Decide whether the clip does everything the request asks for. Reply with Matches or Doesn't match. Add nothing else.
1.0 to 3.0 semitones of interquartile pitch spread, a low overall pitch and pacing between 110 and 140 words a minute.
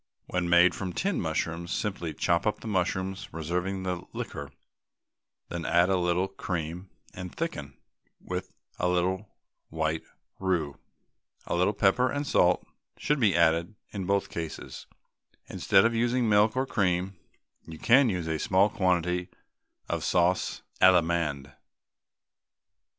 Matches